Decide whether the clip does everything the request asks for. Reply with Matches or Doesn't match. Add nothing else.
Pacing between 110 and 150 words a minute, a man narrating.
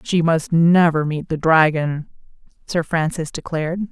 Doesn't match